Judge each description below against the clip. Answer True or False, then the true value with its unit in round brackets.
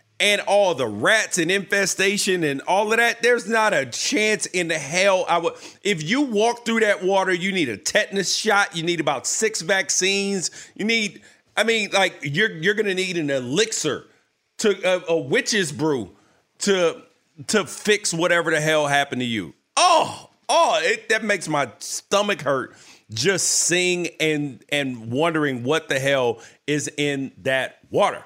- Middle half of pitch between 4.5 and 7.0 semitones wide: True (5.1 semitones)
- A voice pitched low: False (185 Hz)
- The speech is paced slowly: False (170 wpm)